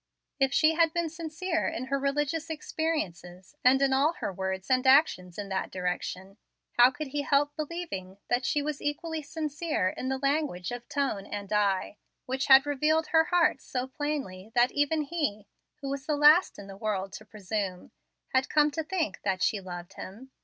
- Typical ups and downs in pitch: No, wide, 7.2 semitones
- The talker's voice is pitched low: No, very high, 270 Hz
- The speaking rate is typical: Yes, average, 185 wpm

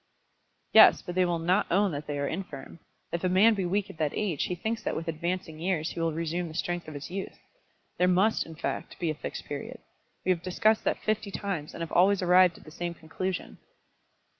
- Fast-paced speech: Yes, fast, 225 wpm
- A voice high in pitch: No, medium, 175 Hz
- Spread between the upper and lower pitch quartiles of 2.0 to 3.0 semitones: Yes, narrow, 2.6 semitones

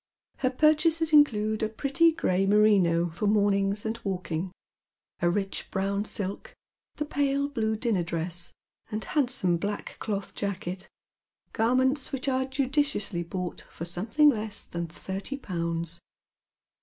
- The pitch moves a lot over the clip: Yes, wide, 6.3 semitones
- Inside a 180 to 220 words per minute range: No, slow, 135 wpm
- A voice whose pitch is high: Yes, high, 210 Hz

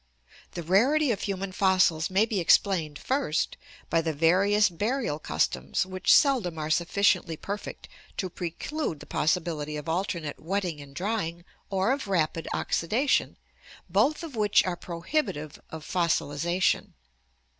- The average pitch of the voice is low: No, medium, 180 Hz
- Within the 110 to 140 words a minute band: Yes, slow, 135 wpm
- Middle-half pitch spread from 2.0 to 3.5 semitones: No, average, 4.2 semitones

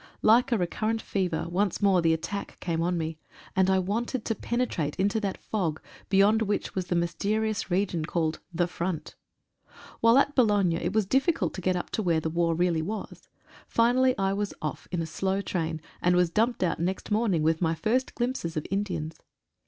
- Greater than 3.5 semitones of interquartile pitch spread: Yes, average, 4.4 semitones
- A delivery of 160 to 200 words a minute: Yes, average, 190 wpm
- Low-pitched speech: No, high, 190 Hz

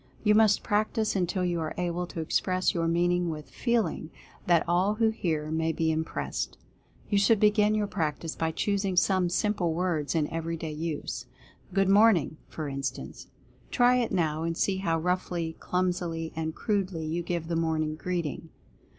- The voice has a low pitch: No, medium, 175 Hz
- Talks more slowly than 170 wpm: No, average, 180 wpm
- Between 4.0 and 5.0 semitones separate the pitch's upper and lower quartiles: No, average, 3.4 semitones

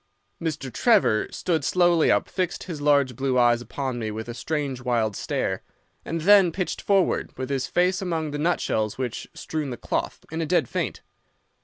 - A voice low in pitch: No, medium, 145 Hz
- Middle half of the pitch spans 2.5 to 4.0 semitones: No, wide, 5.6 semitones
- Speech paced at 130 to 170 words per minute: No, average, 180 wpm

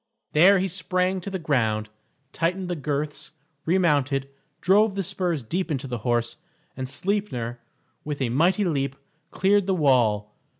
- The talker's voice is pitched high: No, medium, 155 Hz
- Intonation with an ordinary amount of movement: No, wide, 6.2 semitones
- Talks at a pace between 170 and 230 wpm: No, average, 145 wpm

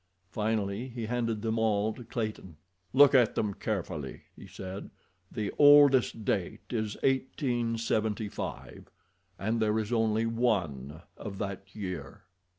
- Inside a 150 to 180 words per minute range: No, slow, 135 wpm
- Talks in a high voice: No, low, 110 Hz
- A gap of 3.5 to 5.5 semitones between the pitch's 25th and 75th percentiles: No, average, 2.9 semitones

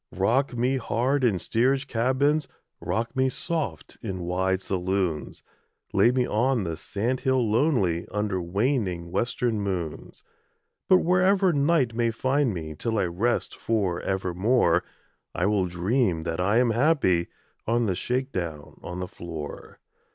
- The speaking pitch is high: No, low, 110 Hz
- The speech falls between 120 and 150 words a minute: Yes, average, 145 wpm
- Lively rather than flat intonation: Yes, wide, 6.3 semitones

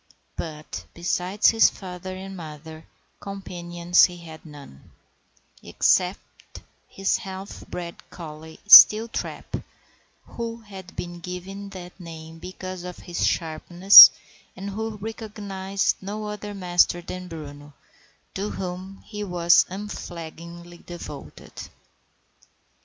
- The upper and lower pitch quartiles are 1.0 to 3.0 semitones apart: Yes, narrow, 2.5 semitones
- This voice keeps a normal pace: No, slow, 105 wpm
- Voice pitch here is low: No, medium, 180 Hz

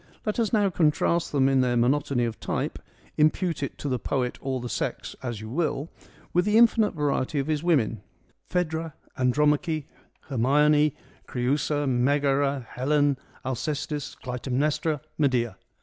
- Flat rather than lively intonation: No, average, 3.2 semitones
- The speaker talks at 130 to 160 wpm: Yes, average, 150 wpm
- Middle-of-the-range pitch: Yes, medium, 145 Hz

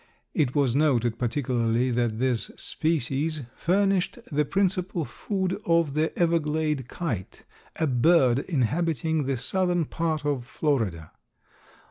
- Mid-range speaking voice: Yes, medium, 150 Hz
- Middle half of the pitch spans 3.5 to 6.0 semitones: Yes, average, 5.1 semitones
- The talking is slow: Yes, slow, 115 wpm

